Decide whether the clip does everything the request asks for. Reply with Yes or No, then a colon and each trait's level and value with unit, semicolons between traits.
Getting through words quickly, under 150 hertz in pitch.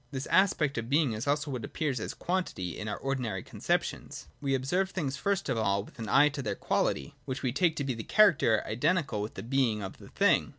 Yes: fast, 230 wpm; low, 135 Hz